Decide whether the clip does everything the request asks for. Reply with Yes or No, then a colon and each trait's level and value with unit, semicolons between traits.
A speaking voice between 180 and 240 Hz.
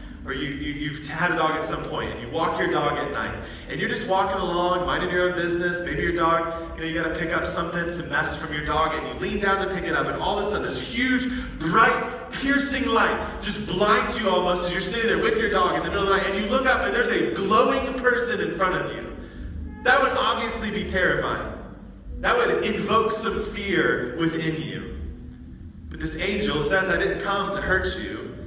Yes: high, 190 Hz